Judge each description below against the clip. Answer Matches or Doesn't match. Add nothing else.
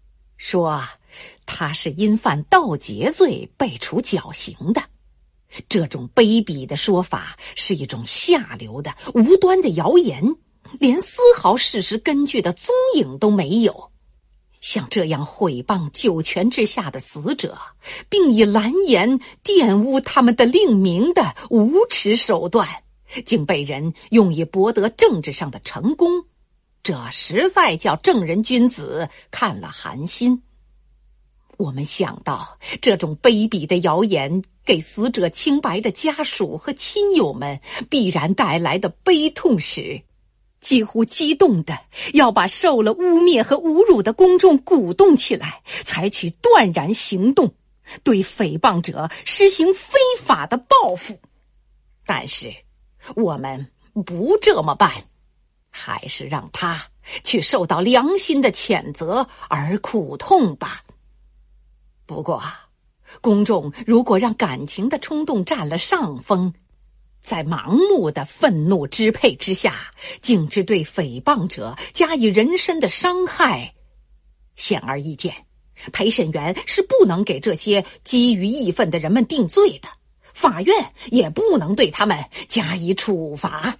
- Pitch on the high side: Matches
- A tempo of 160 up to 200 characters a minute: Matches